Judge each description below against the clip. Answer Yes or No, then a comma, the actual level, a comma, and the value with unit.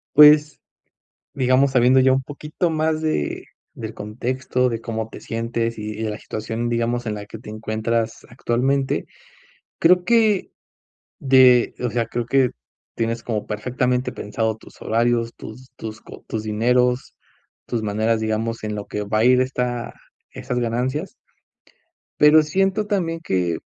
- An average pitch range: Yes, average, 3.0 semitones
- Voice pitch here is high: No, low, 120 Hz